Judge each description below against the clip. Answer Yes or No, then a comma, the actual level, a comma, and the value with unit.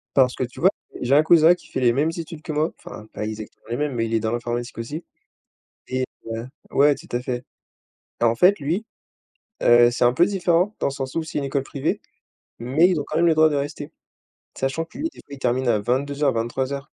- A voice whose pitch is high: No, medium, 140 Hz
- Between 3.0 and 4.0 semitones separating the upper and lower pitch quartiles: No, average, 4.6 semitones